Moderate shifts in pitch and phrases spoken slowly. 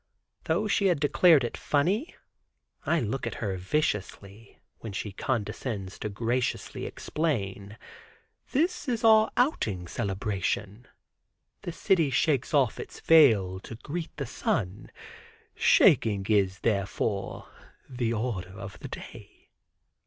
No: wide, 8.0 semitones; slow, 120 wpm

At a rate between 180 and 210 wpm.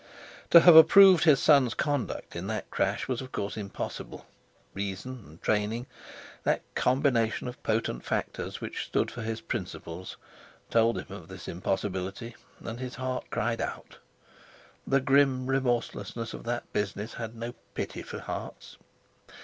No: average, 140 wpm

